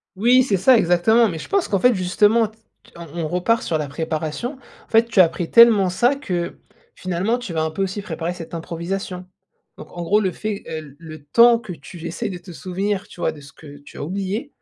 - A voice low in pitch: No, medium, 185 Hz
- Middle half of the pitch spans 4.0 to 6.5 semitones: Yes, average, 4.8 semitones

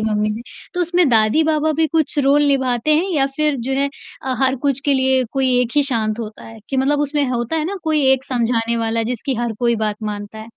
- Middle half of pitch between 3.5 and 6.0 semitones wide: Yes, average, 4.3 semitones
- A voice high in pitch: Yes, very high, 260 Hz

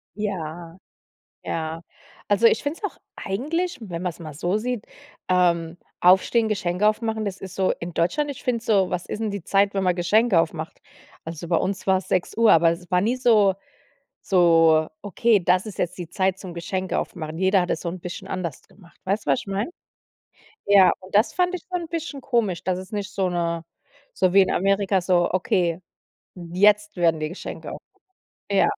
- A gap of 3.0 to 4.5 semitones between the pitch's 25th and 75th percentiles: Yes, average, 3.4 semitones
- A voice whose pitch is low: No, high, 190 Hz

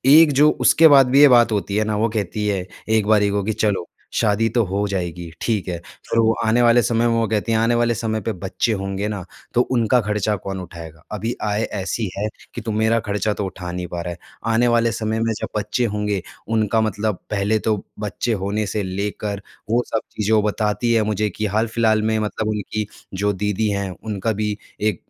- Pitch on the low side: Yes, low, 105 Hz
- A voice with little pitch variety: Yes, narrow, 2.0 semitones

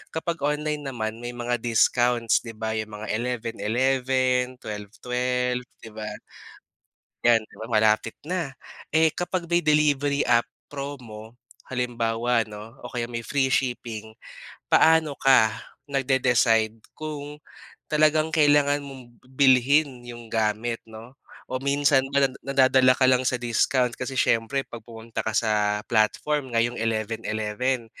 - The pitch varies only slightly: No, average, 3.4 semitones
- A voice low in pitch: Yes, low, 125 Hz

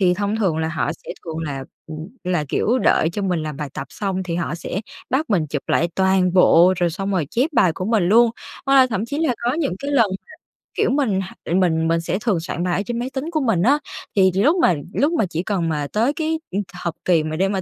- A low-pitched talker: No, high, 190 Hz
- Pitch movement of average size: No, wide, 5.9 semitones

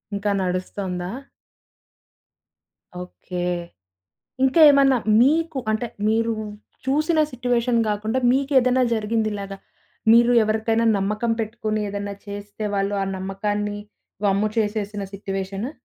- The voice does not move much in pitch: No, average, 3.1 semitones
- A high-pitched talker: Yes, high, 215 Hz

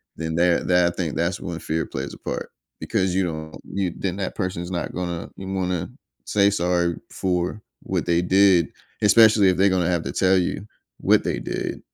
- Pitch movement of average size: No, narrow, 1.9 semitones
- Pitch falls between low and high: No, very low, 90 Hz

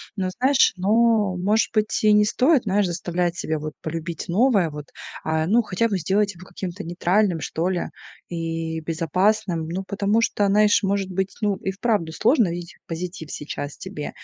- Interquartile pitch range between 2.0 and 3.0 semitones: No, average, 3.9 semitones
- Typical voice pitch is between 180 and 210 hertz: Yes, medium, 185 Hz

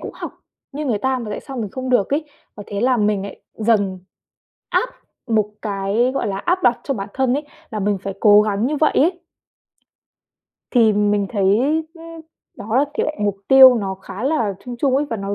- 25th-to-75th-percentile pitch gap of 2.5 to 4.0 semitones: No, average, 4.7 semitones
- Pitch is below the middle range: No, high, 220 Hz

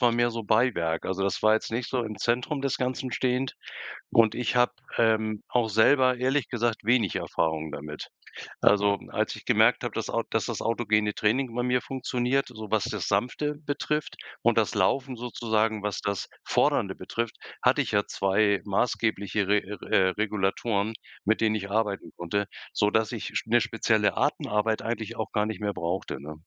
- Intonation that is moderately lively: Yes, average, 3.1 semitones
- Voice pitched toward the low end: Yes, low, 110 Hz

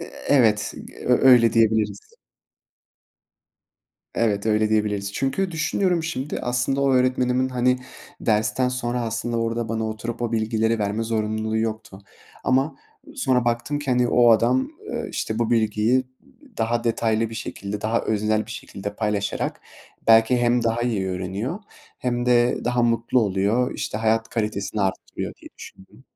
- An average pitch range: No, narrow, 2.3 semitones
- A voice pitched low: Yes, low, 115 Hz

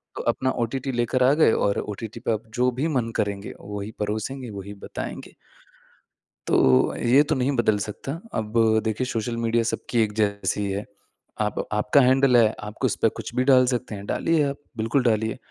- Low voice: Yes, low, 115 Hz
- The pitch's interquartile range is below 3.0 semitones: No, average, 3.4 semitones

